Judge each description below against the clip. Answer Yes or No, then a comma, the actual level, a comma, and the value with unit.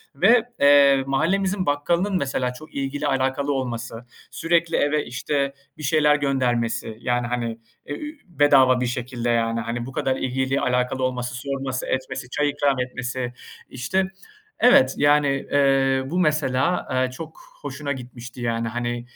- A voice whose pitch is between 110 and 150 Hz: Yes, low, 135 Hz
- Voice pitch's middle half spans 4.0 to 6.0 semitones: No, average, 2.7 semitones